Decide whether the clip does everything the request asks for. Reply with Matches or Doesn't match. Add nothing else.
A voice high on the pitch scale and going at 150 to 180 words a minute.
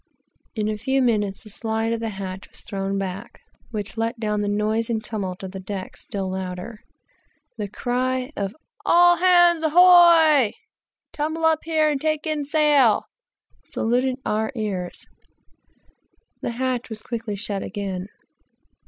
Matches